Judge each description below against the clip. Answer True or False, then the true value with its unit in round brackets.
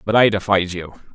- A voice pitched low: True (100 Hz)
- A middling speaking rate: False (210 wpm)